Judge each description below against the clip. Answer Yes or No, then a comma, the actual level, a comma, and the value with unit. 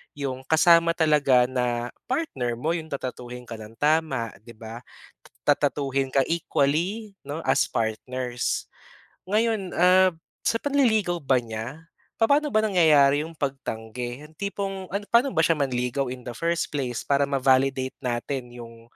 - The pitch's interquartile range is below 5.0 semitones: No, wide, 5.4 semitones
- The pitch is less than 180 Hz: Yes, medium, 140 Hz